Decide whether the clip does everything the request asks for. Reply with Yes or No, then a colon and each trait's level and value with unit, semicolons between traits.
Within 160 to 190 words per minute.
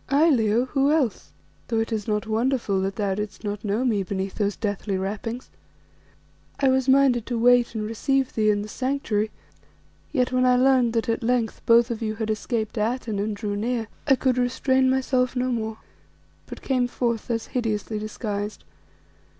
Yes: average, 180 wpm